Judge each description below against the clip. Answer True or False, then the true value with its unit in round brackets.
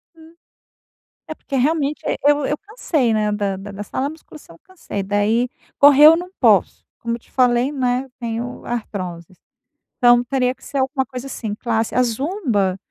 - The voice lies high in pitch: True (250 Hz)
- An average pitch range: True (4.9 semitones)